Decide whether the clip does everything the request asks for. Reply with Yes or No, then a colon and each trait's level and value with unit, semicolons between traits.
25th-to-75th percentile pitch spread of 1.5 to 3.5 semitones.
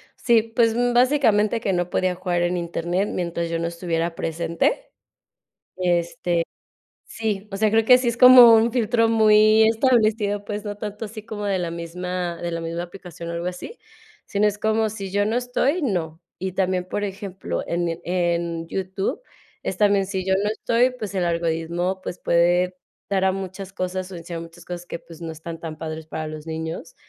No: average, 4.0 semitones